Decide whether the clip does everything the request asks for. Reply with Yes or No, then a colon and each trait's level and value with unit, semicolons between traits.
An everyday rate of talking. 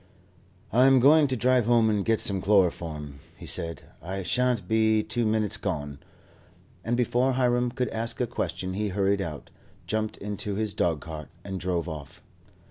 Yes: average, 165 wpm